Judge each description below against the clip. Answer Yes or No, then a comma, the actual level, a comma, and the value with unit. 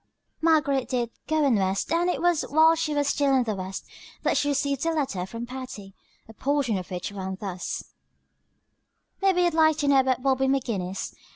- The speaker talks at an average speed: Yes, average, 190 wpm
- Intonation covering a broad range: Yes, wide, 6.3 semitones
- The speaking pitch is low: No, very high, 270 Hz